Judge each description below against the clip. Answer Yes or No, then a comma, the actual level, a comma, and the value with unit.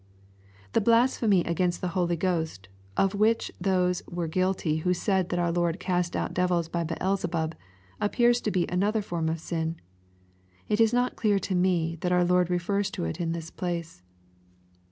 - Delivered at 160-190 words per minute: Yes, average, 175 wpm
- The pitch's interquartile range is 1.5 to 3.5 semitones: Yes, narrow, 2.5 semitones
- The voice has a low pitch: No, medium, 180 Hz